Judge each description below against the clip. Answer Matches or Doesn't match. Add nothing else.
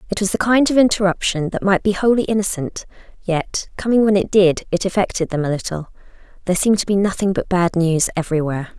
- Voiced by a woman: Matches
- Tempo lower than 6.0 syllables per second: Doesn't match